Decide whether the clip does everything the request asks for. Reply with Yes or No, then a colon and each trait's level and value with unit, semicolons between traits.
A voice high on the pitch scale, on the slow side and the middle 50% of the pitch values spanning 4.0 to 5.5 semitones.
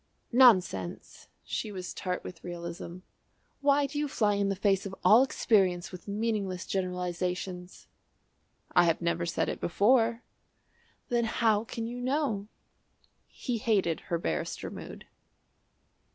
Yes: high, 195 Hz; slow, 130 wpm; average, 4.5 semitones